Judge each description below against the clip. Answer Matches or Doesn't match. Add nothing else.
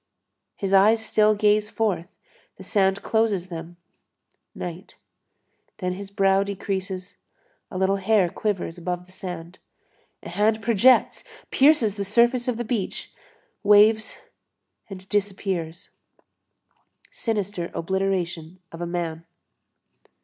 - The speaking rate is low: Matches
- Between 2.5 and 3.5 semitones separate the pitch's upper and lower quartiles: Matches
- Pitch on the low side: Doesn't match